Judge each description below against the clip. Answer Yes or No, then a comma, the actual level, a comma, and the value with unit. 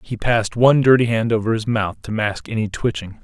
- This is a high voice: No, low, 110 Hz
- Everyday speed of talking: No, fast, 225 wpm